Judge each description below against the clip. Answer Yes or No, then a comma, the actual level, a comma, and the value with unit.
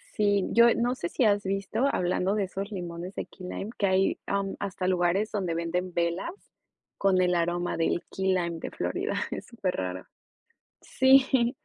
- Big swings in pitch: No, narrow, 2.6 semitones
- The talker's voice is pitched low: No, high, 190 Hz